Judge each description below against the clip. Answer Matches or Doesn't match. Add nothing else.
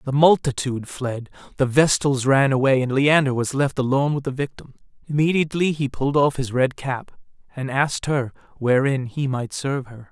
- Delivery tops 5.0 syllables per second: Matches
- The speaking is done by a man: Matches